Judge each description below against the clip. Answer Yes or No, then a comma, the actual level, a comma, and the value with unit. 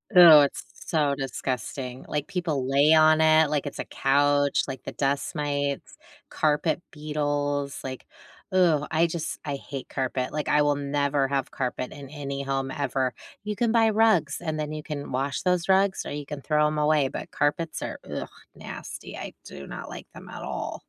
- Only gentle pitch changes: Yes, narrow, 2.2 semitones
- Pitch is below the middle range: No, medium, 145 Hz